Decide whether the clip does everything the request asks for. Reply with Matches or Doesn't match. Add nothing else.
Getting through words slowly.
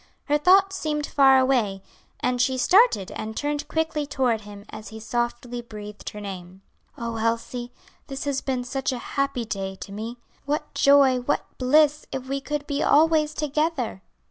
Doesn't match